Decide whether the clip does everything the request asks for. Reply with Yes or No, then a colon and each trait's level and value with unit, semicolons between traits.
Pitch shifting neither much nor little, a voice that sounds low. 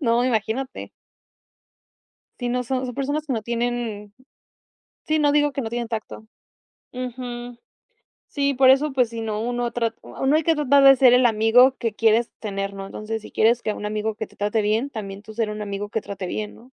No: average, 3.1 semitones; high, 235 Hz